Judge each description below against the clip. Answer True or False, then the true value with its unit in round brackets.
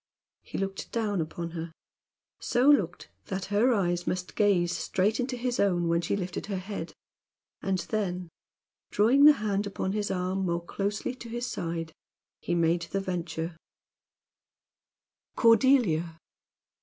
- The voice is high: True (195 Hz)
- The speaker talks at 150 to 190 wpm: False (140 wpm)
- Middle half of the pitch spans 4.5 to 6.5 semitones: False (3.8 semitones)